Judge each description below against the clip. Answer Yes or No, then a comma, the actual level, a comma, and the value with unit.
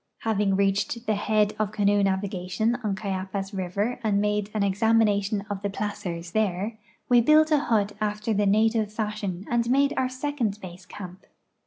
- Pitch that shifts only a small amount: Yes, narrow, 2.2 semitones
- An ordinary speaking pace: Yes, average, 165 wpm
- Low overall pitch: No, high, 210 Hz